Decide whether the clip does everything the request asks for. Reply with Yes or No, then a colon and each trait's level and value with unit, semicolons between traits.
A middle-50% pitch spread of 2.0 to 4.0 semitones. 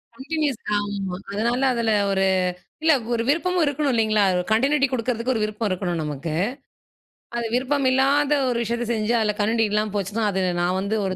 No: average, 4.4 semitones